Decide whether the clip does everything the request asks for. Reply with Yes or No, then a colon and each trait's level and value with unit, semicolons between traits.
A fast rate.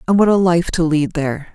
Yes: fast, 270 wpm